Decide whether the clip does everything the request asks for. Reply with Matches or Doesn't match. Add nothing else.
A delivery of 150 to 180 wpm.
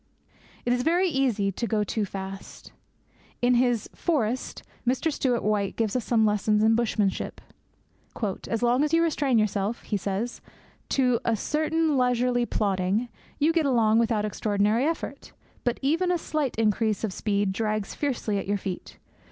Matches